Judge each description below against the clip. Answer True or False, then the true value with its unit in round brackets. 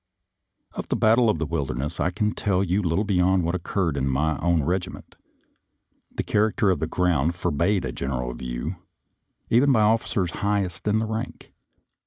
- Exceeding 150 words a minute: True (170 wpm)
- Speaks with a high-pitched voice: False (90 Hz)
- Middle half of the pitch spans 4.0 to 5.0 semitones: True (4.7 semitones)